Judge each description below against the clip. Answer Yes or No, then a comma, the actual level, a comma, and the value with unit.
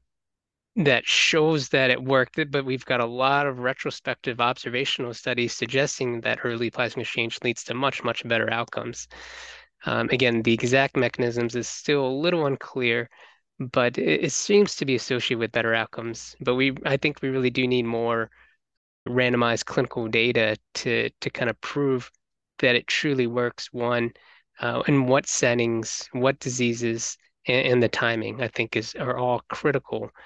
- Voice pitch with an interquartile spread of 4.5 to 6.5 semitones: No, narrow, 2.4 semitones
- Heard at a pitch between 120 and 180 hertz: Yes, low, 125 Hz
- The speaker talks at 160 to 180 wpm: Yes, average, 165 wpm